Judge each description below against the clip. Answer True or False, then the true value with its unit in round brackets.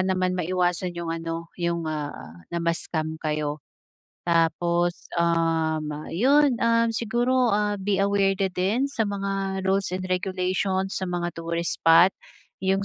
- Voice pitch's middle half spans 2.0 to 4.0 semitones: True (2.6 semitones)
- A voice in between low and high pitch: True (180 Hz)